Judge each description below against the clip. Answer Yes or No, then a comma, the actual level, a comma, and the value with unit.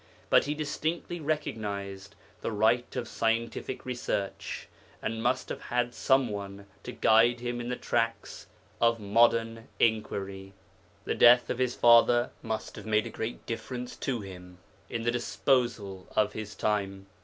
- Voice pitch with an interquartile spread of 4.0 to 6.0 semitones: No, average, 2.7 semitones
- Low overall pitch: Yes, low, 115 Hz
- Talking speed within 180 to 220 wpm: No, average, 150 wpm